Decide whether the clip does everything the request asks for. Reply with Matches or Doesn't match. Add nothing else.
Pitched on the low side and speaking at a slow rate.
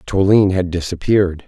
Matches